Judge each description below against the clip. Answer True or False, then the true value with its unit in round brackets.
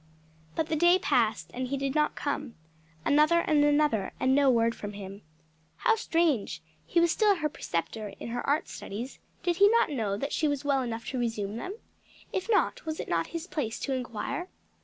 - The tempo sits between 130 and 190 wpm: False (200 wpm)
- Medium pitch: False (280 Hz)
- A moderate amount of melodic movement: False (5.9 semitones)